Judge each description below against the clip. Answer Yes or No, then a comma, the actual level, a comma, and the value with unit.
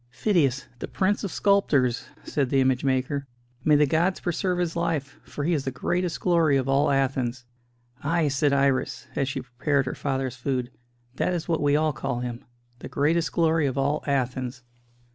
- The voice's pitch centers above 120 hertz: Yes, medium, 140 Hz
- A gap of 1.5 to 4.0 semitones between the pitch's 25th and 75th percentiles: Yes, average, 3.7 semitones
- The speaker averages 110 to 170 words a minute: No, average, 180 wpm